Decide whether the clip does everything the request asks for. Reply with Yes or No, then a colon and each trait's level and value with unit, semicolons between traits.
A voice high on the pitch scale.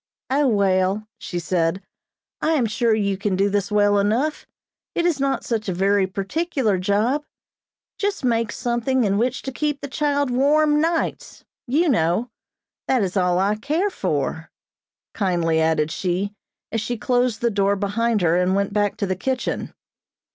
Yes: high, 210 Hz